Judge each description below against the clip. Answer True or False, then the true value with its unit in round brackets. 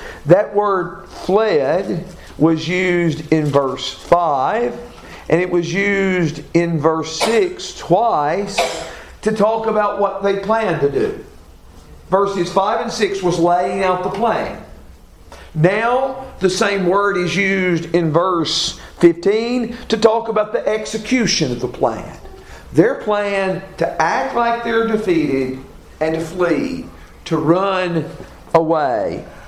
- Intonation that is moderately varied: True (4.6 semitones)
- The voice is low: False (185 Hz)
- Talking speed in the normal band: False (130 wpm)